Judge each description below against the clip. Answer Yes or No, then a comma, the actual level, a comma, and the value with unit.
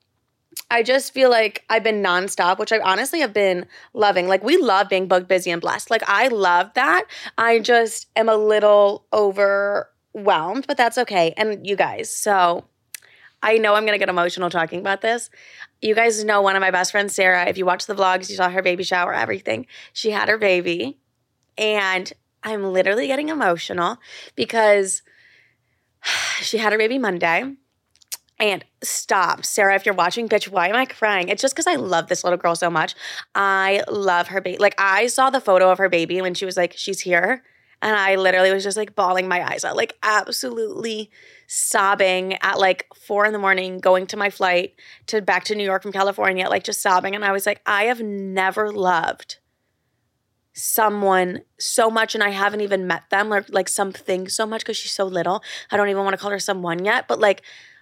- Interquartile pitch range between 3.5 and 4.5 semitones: No, average, 2.7 semitones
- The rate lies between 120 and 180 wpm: No, average, 200 wpm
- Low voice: No, high, 200 Hz